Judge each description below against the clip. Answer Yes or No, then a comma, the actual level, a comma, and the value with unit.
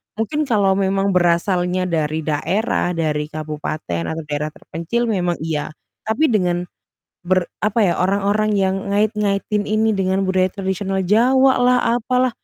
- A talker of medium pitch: No, high, 195 Hz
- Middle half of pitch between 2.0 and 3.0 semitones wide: No, average, 3.8 semitones